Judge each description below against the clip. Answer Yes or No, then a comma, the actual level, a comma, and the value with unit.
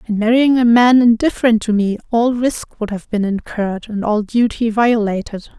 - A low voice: No, high, 225 Hz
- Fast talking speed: No, average, 185 wpm